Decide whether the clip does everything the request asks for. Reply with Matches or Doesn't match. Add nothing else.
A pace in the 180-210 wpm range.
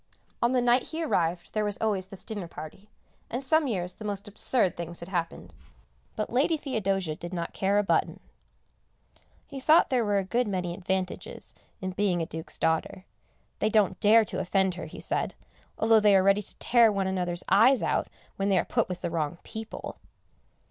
Matches